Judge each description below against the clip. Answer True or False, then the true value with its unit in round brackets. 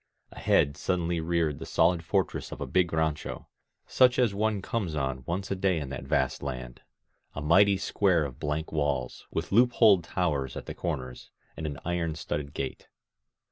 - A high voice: False (80 Hz)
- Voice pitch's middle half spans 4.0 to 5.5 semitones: True (4.4 semitones)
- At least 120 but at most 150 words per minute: False (180 wpm)